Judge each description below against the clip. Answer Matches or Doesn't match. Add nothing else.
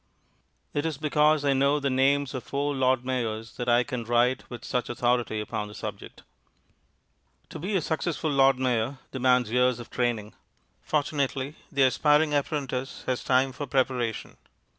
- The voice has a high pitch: Doesn't match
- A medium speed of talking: Matches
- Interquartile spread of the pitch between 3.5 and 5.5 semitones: Doesn't match